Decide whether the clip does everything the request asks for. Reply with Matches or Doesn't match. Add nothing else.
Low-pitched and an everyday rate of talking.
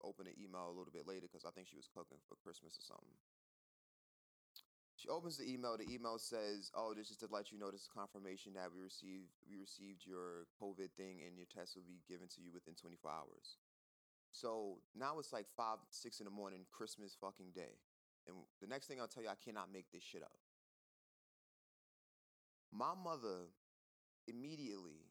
Matches